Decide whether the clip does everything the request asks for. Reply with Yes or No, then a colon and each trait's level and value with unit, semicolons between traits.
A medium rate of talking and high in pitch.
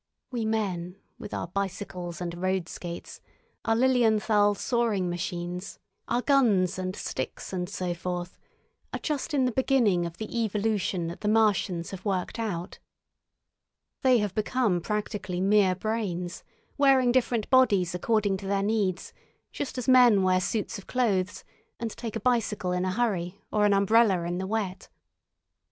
Yes: average, 155 wpm; high, 200 Hz